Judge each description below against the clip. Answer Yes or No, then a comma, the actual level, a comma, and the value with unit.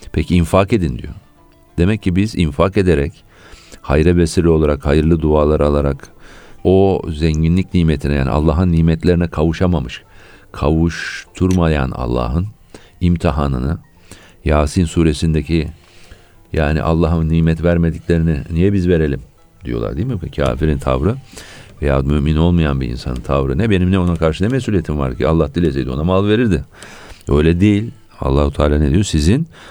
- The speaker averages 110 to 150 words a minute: Yes, average, 135 wpm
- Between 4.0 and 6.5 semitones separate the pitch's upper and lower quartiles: No, average, 3.4 semitones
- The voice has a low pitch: Yes, very low, 80 Hz